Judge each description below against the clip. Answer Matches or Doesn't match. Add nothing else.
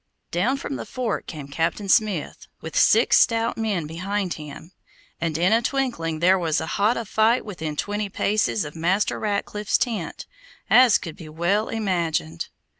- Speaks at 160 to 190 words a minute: Matches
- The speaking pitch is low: Doesn't match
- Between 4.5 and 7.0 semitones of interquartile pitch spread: Matches